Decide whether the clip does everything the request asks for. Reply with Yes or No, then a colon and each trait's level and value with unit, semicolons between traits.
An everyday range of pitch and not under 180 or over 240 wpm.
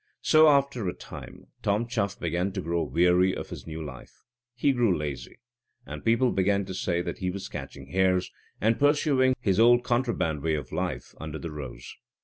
No: wide, 6.8 semitones; average, 185 wpm